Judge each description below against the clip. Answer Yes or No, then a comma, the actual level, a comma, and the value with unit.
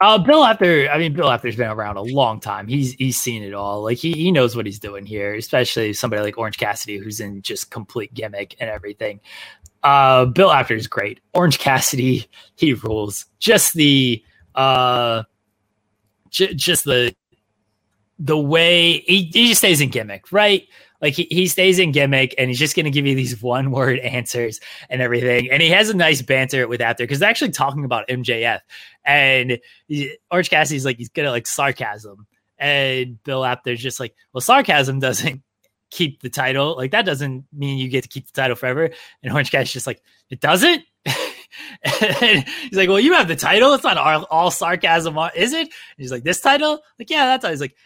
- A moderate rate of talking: Yes, average, 190 wpm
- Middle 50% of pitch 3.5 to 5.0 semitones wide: No, wide, 5.6 semitones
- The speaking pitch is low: Yes, low, 130 Hz